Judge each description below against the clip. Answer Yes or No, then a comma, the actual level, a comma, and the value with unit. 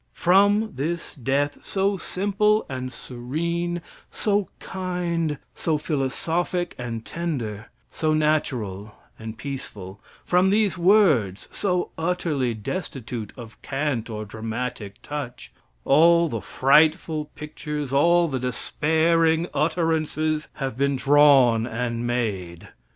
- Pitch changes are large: Yes, wide, 5.8 semitones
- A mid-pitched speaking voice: Yes, medium, 150 Hz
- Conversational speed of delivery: No, slow, 105 wpm